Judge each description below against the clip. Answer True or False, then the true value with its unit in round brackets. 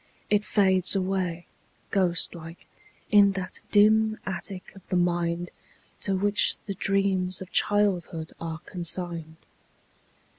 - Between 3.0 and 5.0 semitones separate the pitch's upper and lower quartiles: False (2.4 semitones)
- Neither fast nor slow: False (115 wpm)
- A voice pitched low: False (185 Hz)